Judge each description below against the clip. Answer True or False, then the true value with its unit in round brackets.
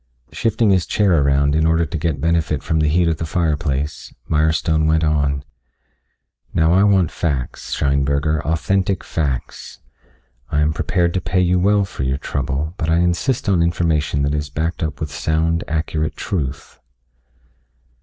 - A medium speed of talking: True (160 wpm)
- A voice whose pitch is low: True (80 Hz)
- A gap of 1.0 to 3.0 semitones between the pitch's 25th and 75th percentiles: True (2.6 semitones)